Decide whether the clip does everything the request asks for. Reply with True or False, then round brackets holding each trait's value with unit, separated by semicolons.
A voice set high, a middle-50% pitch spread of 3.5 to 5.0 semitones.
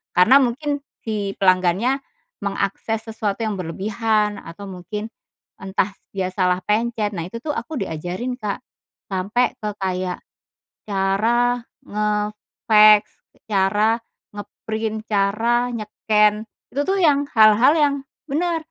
False (210 Hz; 3.1 semitones)